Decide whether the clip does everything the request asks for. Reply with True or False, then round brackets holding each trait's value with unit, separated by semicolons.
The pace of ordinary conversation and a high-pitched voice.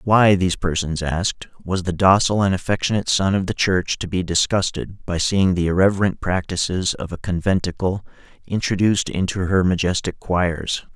False (160 wpm; 90 Hz)